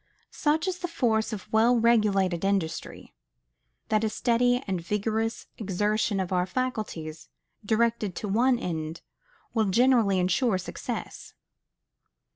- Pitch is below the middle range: No, high, 215 Hz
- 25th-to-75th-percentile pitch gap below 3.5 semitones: No, average, 3.9 semitones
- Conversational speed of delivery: No, slow, 120 wpm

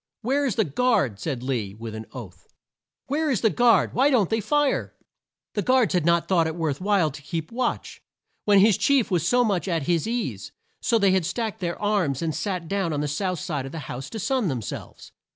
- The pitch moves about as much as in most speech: No, wide, 7.1 semitones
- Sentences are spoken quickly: Yes, fast, 225 wpm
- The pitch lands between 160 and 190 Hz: Yes, medium, 185 Hz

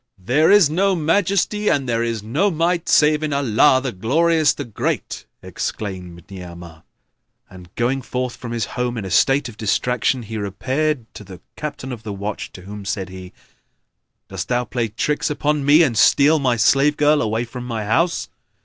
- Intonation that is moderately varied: No, wide, 6.0 semitones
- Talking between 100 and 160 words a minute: No, average, 180 wpm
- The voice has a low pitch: Yes, low, 125 Hz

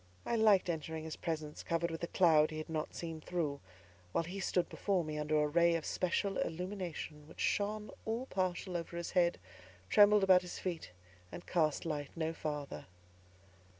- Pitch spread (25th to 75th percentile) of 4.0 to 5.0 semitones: No, average, 2.9 semitones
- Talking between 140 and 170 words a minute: No, average, 180 wpm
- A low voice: No, medium, 170 Hz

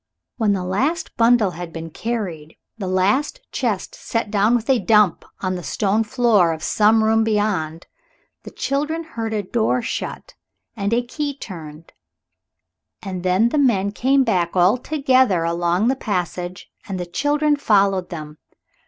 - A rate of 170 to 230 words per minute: No, average, 155 wpm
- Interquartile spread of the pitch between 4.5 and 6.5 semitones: Yes, average, 4.9 semitones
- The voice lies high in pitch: Yes, high, 210 Hz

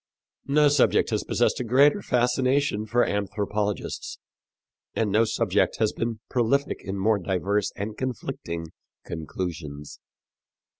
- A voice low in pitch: Yes, low, 110 Hz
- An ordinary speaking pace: No, slow, 115 wpm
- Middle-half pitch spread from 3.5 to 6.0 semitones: Yes, average, 4.2 semitones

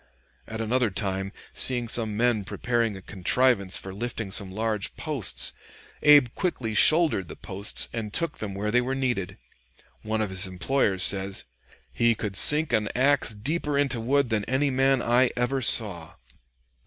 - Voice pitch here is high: No, low, 115 Hz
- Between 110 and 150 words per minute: No, average, 160 wpm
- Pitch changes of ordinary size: Yes, average, 4.6 semitones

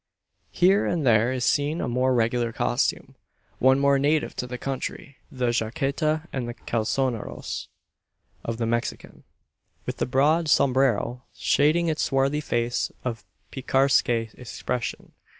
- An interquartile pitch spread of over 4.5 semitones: No, average, 3.2 semitones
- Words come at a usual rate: No, slow, 130 wpm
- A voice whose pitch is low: Yes, low, 130 Hz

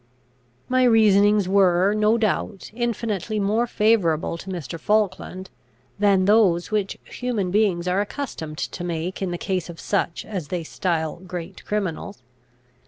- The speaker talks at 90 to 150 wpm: Yes, average, 140 wpm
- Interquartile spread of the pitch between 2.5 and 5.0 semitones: Yes, average, 3.3 semitones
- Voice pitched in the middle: No, high, 195 Hz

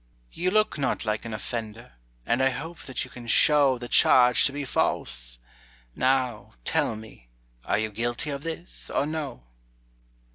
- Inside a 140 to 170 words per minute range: Yes, average, 160 wpm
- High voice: No, low, 125 Hz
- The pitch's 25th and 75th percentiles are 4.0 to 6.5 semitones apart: Yes, average, 4.6 semitones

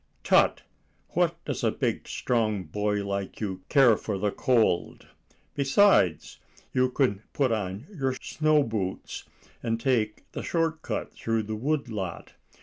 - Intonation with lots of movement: No, average, 4.9 semitones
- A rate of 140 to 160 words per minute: Yes, average, 145 wpm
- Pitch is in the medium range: No, low, 115 Hz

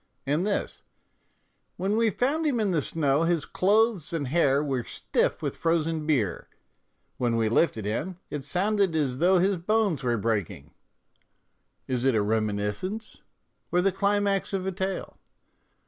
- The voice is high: No, medium, 165 Hz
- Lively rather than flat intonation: Yes, wide, 6.9 semitones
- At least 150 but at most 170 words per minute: Yes, average, 160 wpm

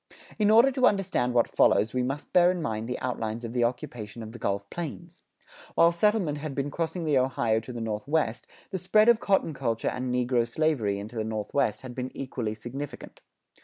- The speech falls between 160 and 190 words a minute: No, average, 200 wpm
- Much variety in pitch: Yes, wide, 6.3 semitones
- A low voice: Yes, low, 130 Hz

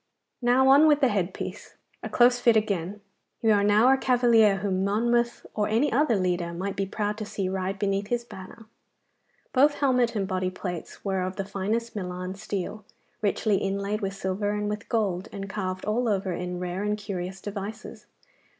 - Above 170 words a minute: Yes, average, 185 wpm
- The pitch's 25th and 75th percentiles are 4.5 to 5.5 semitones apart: No, average, 3.1 semitones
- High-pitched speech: Yes, high, 205 Hz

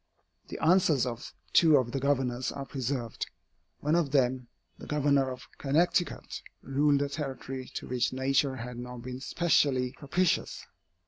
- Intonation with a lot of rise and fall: No, narrow, 2.5 semitones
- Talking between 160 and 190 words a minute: No, average, 145 wpm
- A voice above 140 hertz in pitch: No, low, 135 Hz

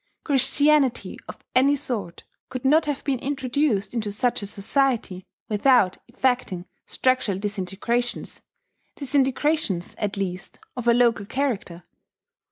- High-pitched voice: Yes, high, 245 Hz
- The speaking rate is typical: No, slow, 115 wpm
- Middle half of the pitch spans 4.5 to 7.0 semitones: Yes, average, 5.2 semitones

